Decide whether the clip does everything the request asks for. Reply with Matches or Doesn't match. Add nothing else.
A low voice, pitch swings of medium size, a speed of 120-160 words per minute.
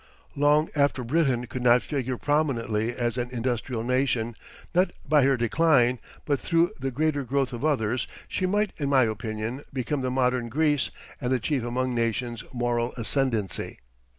Matches